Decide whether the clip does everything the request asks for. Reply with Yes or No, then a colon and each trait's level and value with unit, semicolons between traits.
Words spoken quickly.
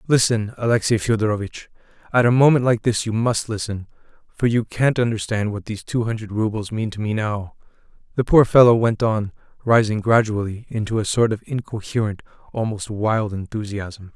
No: average, 165 wpm